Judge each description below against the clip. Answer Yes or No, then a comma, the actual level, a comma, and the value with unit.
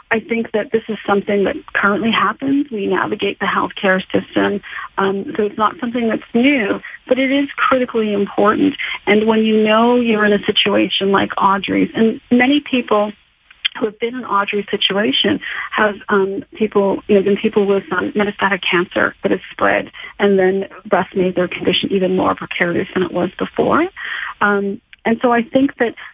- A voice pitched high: Yes, high, 210 Hz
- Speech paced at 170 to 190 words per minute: Yes, average, 180 wpm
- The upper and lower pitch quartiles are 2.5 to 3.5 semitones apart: Yes, average, 3.2 semitones